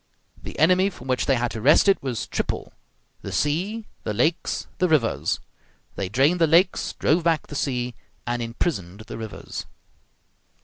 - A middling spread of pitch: No, wide, 6.2 semitones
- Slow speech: No, average, 165 wpm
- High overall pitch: No, medium, 140 Hz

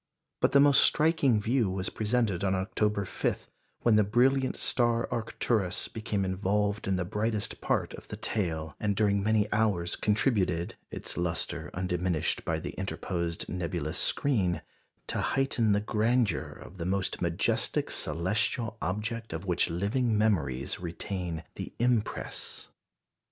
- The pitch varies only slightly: No, average, 4.0 semitones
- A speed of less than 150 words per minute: Yes, average, 140 wpm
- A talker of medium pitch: No, low, 100 Hz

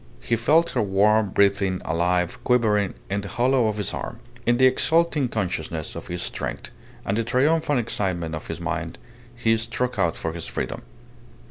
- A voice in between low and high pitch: No, low, 105 Hz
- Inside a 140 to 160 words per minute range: No, average, 170 wpm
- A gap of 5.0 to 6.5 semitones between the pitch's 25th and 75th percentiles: Yes, average, 5.3 semitones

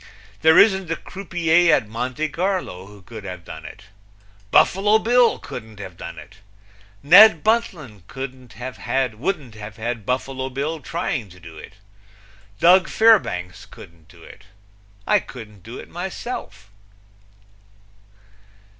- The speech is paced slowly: Yes, slow, 125 wpm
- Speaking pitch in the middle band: No, low, 130 Hz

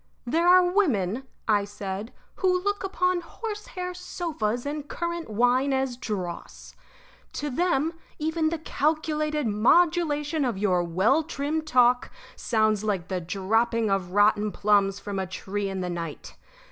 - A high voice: Yes, high, 245 Hz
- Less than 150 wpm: Yes, average, 140 wpm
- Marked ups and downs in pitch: Yes, wide, 7.9 semitones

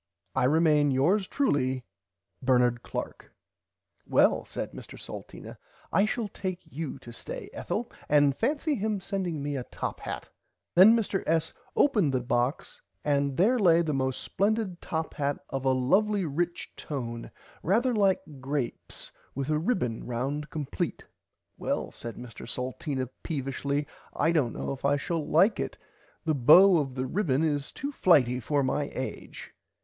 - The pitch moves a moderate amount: No, wide, 5.9 semitones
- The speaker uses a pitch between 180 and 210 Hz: No, medium, 150 Hz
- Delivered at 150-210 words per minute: Yes, average, 155 wpm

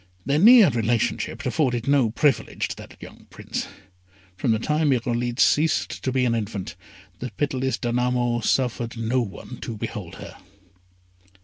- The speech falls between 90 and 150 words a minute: Yes, average, 145 wpm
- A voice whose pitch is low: Yes, low, 125 Hz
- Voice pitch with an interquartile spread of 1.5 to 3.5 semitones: Yes, average, 2.7 semitones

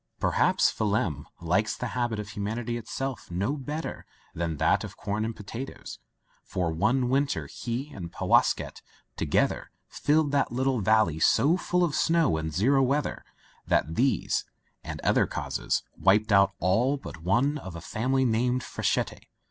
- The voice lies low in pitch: Yes, low, 115 Hz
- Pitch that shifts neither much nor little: No, wide, 5.7 semitones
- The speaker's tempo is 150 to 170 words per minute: Yes, average, 165 wpm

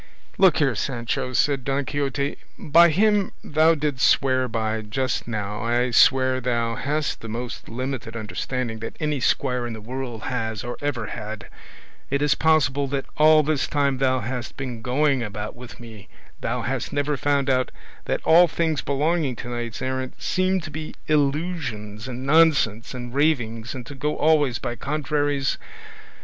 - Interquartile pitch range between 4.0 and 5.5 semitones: No, average, 3.6 semitones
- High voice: No, low, 130 Hz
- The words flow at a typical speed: Yes, average, 165 wpm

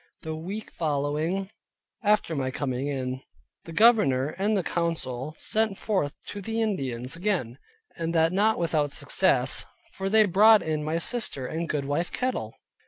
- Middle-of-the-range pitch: Yes, medium, 165 Hz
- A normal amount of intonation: No, wide, 6.1 semitones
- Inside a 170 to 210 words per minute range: No, average, 145 wpm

